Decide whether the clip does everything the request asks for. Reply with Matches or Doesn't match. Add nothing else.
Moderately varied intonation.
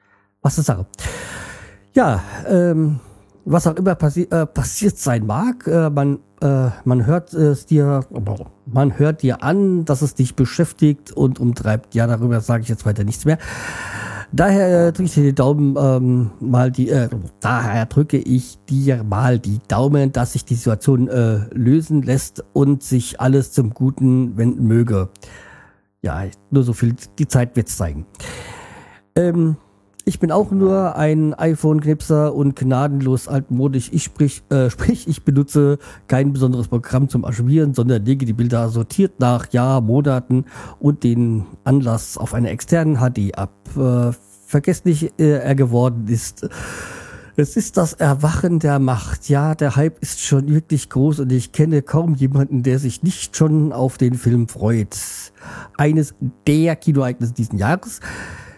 Matches